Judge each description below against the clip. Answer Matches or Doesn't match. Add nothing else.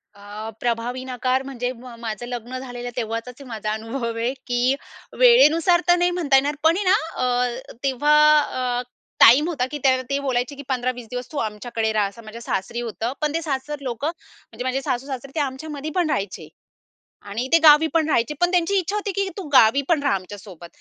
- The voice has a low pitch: Doesn't match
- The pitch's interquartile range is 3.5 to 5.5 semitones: Matches